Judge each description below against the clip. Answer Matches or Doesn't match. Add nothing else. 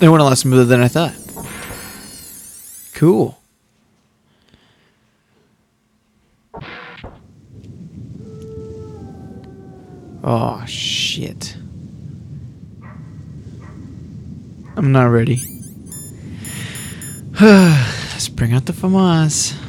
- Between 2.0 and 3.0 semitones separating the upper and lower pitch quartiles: Doesn't match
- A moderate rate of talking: Doesn't match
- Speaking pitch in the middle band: Doesn't match